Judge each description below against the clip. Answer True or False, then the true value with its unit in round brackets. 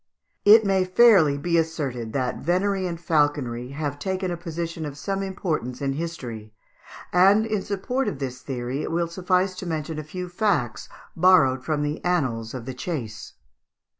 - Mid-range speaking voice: True (160 Hz)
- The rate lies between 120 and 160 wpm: False (170 wpm)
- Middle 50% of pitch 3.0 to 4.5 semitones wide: False (5.5 semitones)